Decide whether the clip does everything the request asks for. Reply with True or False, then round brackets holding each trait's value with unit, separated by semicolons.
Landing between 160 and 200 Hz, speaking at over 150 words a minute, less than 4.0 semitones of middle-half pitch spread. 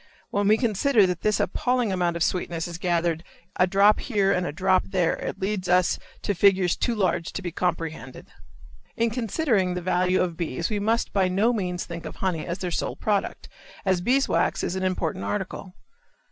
True (185 Hz; 190 wpm; 2.8 semitones)